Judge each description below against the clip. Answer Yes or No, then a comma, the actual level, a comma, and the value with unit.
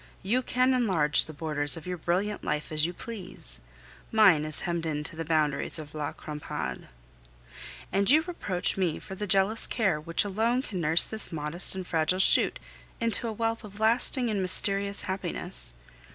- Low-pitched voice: No, medium, 185 Hz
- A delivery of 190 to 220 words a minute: No, average, 175 wpm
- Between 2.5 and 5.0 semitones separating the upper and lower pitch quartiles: No, wide, 5.5 semitones